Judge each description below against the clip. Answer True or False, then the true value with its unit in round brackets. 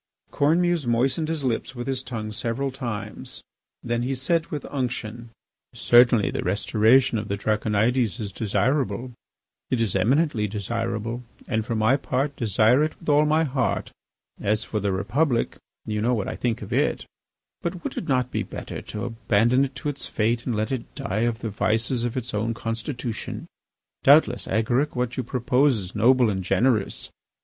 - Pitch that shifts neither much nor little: True (3.5 semitones)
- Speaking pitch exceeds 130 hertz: False (120 Hz)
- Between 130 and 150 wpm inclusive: False (175 wpm)